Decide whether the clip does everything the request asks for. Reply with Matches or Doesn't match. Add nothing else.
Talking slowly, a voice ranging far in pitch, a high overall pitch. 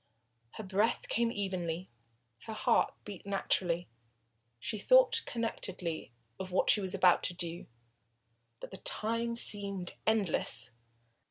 Doesn't match